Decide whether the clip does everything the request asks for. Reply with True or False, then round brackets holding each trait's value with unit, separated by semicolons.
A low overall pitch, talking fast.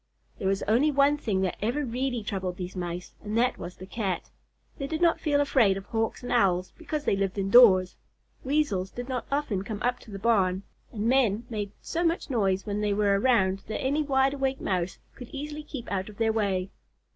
False (220 Hz; 210 wpm)